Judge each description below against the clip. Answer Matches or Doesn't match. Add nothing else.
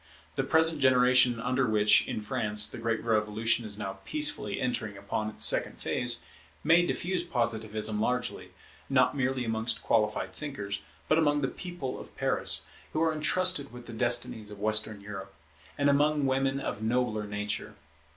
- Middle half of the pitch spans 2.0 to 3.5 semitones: Doesn't match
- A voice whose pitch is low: Matches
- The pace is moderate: Matches